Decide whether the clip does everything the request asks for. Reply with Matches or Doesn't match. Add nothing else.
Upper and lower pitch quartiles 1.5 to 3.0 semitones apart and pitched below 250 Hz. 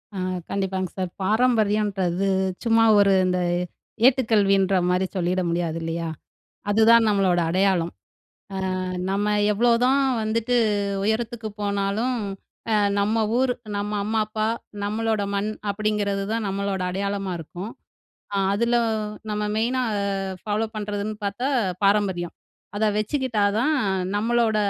Matches